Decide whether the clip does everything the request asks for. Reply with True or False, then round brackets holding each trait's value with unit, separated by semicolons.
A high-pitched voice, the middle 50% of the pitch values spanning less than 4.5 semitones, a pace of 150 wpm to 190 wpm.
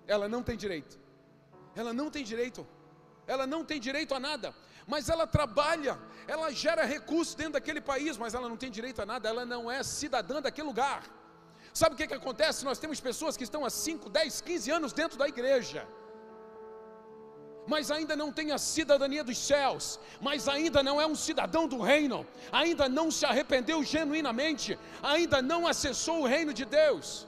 True (280 Hz; 3.8 semitones; 180 wpm)